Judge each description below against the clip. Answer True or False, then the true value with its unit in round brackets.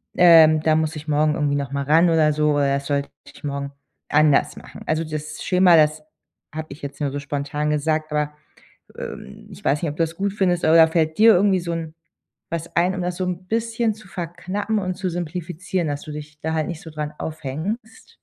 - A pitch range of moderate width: True (3.0 semitones)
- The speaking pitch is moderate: True (160 Hz)